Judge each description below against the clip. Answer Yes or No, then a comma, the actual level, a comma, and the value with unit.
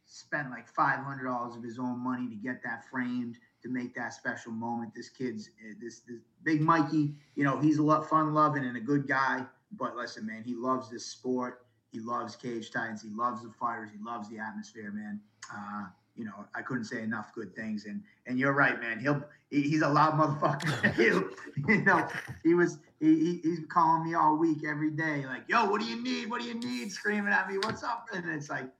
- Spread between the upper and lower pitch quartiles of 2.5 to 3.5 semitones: No, average, 5.0 semitones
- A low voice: Yes, low, 130 Hz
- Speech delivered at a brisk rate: Yes, fast, 220 wpm